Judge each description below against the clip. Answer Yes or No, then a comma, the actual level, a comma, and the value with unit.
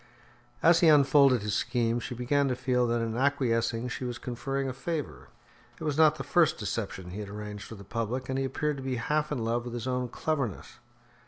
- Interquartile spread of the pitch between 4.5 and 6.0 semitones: No, average, 3.3 semitones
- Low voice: Yes, low, 125 Hz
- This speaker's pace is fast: Yes, fast, 220 wpm